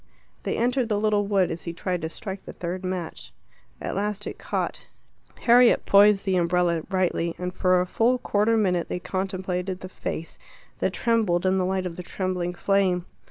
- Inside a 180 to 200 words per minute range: Yes, average, 185 wpm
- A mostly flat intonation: Yes, narrow, 2.3 semitones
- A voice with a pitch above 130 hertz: Yes, medium, 185 Hz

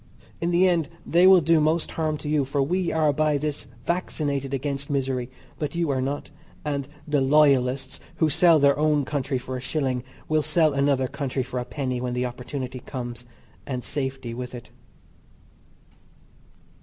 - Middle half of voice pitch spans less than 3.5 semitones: Yes, average, 3.0 semitones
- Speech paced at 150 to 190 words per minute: Yes, average, 170 wpm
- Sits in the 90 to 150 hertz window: Yes, medium, 140 Hz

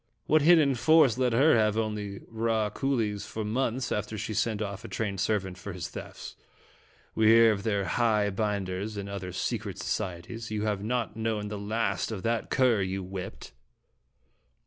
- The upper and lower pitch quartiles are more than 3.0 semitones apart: No, narrow, 2.5 semitones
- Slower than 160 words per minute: No, average, 175 wpm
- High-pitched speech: No, low, 110 Hz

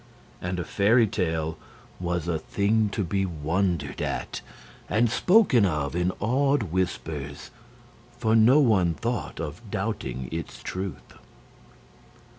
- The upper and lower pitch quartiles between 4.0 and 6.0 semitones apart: Yes, average, 5.1 semitones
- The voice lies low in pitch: Yes, very low, 95 Hz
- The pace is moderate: No, slow, 120 wpm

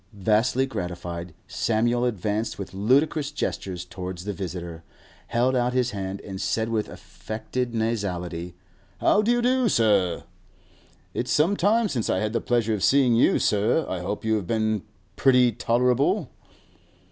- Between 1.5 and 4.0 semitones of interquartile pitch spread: No, average, 4.9 semitones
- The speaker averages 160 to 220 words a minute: No, average, 150 wpm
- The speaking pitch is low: Yes, low, 110 Hz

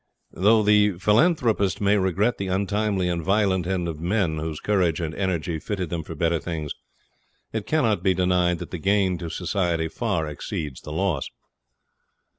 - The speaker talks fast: No, average, 165 wpm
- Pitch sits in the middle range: No, very low, 90 Hz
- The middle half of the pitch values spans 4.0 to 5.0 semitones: No, average, 3.5 semitones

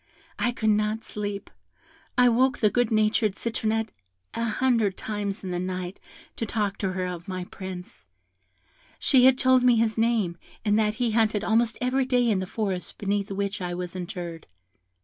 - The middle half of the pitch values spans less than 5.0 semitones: Yes, average, 3.6 semitones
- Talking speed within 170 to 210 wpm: Yes, average, 175 wpm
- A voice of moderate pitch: No, high, 210 Hz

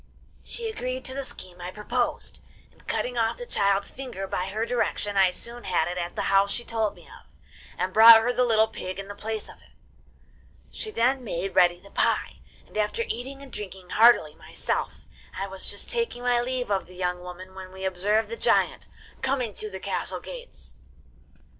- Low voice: No, high, 215 Hz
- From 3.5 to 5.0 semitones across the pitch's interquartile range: Yes, average, 4.6 semitones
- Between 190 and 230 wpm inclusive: Yes, average, 195 wpm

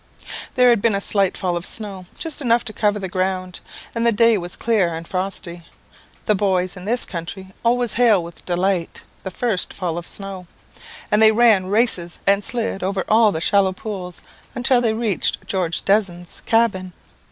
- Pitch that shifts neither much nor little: Yes, average, 3.6 semitones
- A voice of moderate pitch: No, high, 195 Hz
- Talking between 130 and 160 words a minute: No, average, 180 wpm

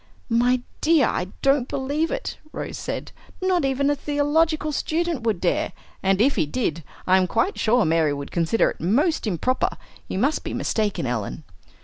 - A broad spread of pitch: Yes, wide, 8.2 semitones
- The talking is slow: No, average, 170 wpm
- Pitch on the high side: Yes, very high, 255 Hz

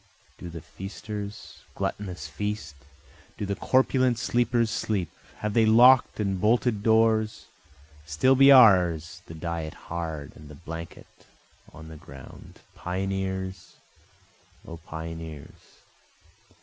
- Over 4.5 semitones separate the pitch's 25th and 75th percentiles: Yes, average, 5.1 semitones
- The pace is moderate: No, slow, 110 wpm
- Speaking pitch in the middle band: No, very low, 95 Hz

